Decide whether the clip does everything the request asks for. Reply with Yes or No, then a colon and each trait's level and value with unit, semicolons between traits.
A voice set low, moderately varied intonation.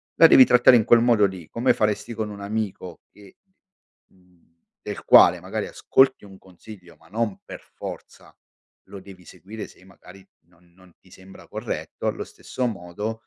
Yes: low, 100 Hz; average, 3.4 semitones